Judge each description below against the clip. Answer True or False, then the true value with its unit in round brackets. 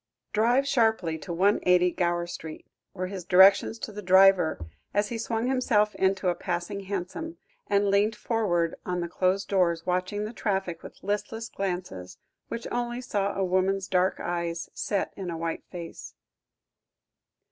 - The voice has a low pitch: False (190 Hz)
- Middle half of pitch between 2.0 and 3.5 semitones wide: True (3.0 semitones)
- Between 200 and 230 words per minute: False (155 wpm)